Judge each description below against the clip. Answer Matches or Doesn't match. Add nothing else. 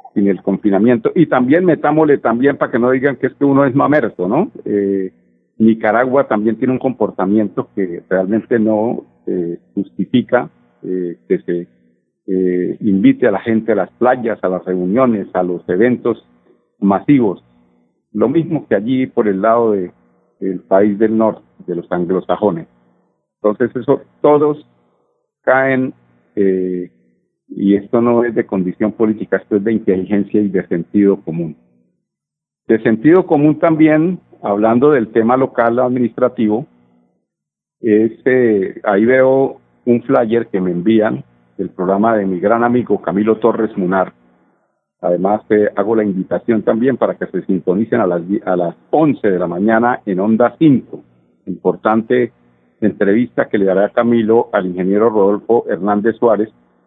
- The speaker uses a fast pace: Doesn't match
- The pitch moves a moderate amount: Matches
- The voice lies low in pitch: Matches